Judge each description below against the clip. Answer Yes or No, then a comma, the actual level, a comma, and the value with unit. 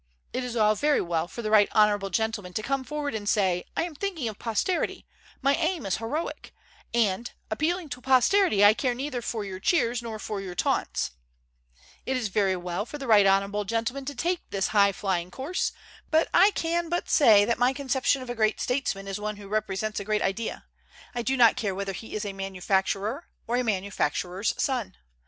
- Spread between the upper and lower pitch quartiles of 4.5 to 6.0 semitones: Yes, average, 5.0 semitones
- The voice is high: Yes, high, 220 Hz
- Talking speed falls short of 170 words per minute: No, average, 200 wpm